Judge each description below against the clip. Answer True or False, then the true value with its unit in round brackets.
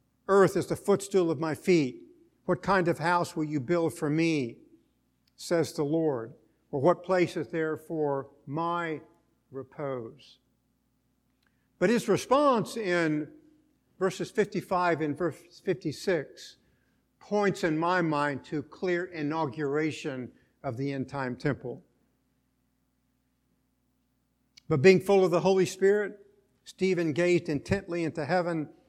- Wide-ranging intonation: False (4.0 semitones)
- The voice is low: False (165 Hz)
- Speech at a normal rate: False (125 wpm)